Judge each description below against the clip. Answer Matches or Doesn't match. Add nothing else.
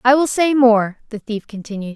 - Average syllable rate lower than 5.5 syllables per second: Matches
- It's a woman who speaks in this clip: Matches